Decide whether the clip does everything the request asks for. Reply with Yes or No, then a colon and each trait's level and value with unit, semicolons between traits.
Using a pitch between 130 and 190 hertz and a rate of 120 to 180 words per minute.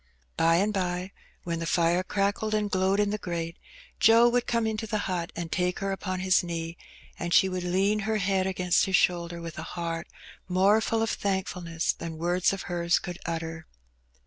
No: medium, 185 Hz; average, 195 wpm